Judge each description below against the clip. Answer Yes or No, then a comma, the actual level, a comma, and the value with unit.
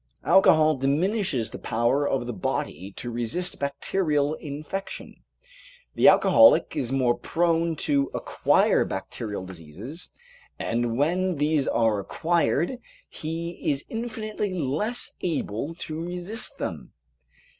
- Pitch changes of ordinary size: No, wide, 6.3 semitones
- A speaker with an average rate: No, slow, 115 wpm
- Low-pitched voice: No, medium, 150 Hz